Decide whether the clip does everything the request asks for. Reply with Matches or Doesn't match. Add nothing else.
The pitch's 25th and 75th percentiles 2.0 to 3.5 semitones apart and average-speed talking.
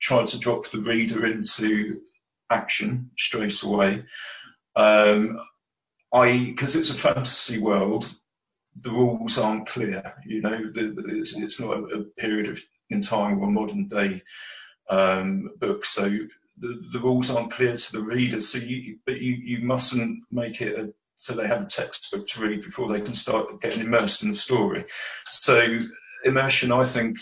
Matches